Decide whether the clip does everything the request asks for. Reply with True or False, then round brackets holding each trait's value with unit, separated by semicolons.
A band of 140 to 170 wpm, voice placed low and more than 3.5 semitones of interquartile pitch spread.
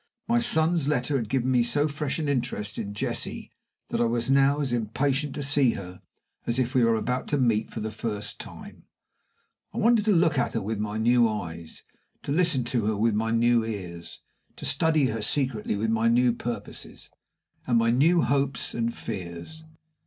False (190 wpm; 120 Hz; 4.3 semitones)